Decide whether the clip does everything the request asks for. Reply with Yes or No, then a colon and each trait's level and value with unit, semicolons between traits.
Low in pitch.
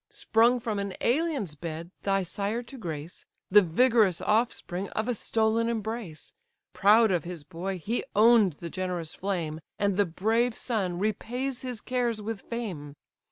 No: high, 205 Hz